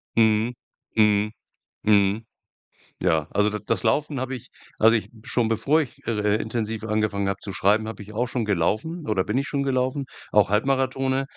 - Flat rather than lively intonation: No, average, 3.7 semitones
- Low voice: Yes, low, 110 Hz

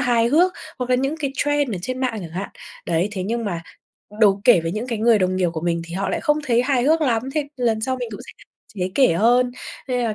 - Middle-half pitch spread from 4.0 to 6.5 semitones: Yes, average, 5.0 semitones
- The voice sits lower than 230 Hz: No, high, 235 Hz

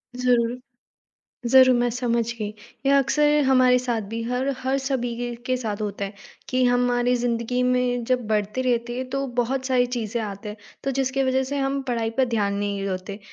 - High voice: Yes, high, 245 Hz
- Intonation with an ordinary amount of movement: No, narrow, 2.3 semitones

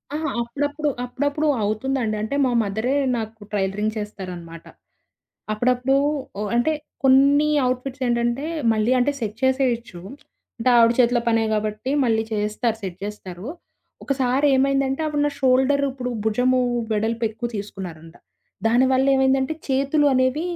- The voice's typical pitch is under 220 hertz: No, high, 245 Hz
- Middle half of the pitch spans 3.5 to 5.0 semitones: Yes, average, 3.8 semitones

